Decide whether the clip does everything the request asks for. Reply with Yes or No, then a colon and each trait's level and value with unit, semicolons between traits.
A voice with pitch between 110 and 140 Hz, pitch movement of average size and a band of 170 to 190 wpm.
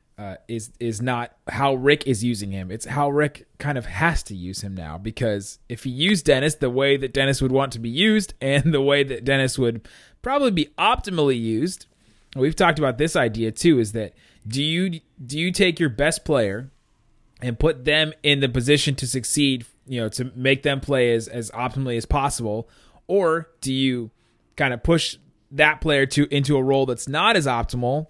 No: low, 135 Hz; average, 4.0 semitones; average, 200 wpm